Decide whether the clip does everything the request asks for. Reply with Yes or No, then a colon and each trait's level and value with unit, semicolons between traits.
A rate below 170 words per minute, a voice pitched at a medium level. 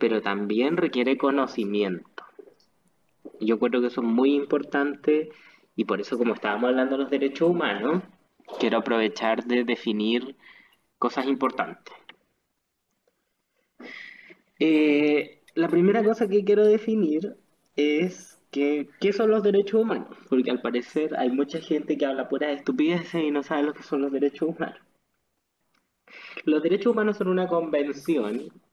Yes: average, 140 wpm; medium, 145 Hz